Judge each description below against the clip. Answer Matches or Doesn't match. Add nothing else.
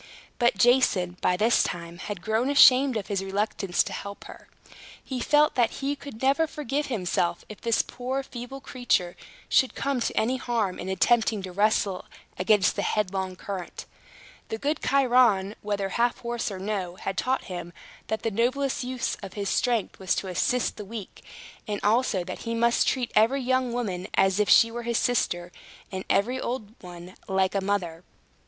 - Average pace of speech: Matches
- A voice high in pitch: Matches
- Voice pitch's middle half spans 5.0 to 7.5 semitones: Doesn't match